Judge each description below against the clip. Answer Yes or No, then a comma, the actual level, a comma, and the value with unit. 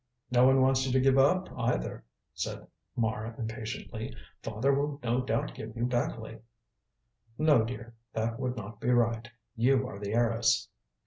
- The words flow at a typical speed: Yes, average, 155 wpm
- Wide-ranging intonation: No, narrow, 2.5 semitones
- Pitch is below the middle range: Yes, low, 120 Hz